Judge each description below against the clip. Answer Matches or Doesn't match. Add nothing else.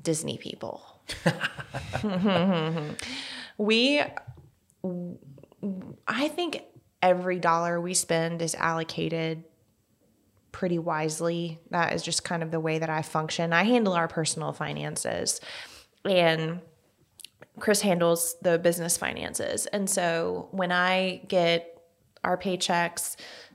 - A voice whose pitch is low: Doesn't match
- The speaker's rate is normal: Doesn't match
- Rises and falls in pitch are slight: Matches